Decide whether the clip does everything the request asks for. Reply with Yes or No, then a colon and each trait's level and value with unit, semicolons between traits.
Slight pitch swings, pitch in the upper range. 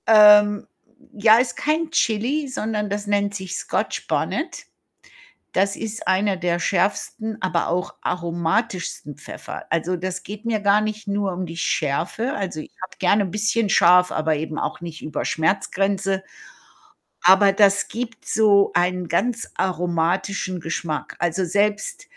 No: average, 3.1 semitones; high, 195 Hz